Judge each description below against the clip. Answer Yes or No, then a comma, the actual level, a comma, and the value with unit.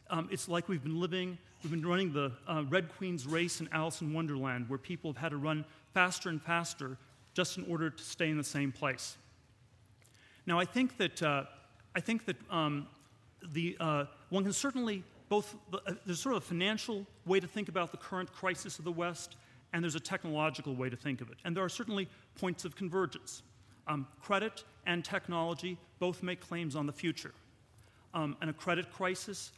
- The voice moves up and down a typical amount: Yes, average, 4.3 semitones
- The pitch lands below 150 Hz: No, medium, 170 Hz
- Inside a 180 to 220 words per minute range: Yes, average, 200 wpm